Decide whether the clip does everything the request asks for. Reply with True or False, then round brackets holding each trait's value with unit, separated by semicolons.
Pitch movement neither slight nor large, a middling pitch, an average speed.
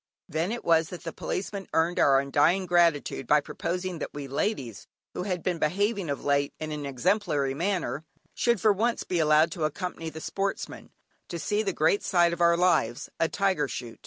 True (4.0 semitones; 170 Hz; 190 wpm)